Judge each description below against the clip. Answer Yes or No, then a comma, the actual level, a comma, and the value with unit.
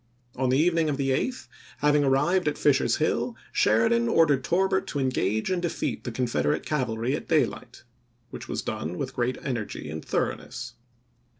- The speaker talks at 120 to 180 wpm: Yes, average, 170 wpm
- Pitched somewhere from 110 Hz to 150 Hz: Yes, low, 135 Hz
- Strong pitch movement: No, average, 4.5 semitones